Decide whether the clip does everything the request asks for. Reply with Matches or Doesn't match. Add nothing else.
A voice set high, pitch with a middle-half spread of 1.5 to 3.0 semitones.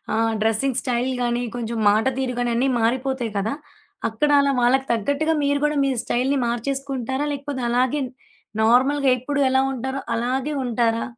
Matches